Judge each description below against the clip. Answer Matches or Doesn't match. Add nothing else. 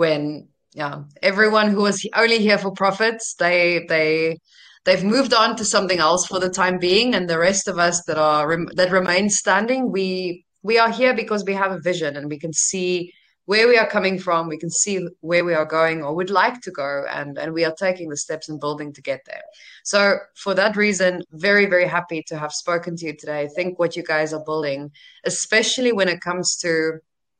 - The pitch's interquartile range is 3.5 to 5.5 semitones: Matches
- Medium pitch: Matches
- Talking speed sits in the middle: Doesn't match